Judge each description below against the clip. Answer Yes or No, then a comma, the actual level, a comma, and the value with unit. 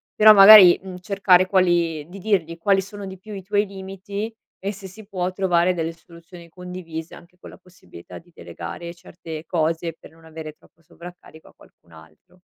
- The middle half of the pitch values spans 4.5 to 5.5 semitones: No, average, 2.8 semitones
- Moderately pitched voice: Yes, medium, 180 Hz